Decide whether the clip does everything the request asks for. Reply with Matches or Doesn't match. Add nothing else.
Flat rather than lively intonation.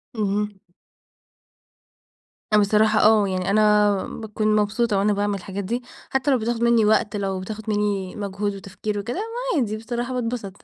Matches